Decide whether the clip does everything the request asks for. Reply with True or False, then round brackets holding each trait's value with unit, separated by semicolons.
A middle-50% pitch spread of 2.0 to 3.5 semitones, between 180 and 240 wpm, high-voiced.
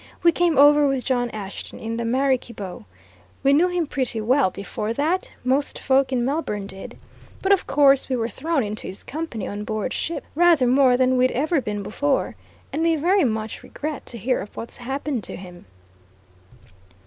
False (4.7 semitones; 185 wpm; 260 Hz)